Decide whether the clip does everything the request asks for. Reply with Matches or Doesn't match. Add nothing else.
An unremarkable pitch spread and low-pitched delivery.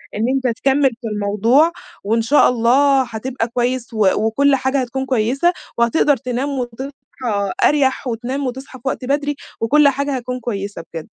Doesn't match